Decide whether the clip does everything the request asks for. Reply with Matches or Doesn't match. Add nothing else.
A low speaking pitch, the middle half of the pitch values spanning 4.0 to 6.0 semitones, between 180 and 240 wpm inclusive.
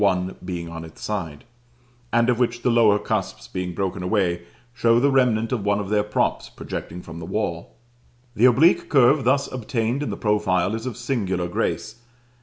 Matches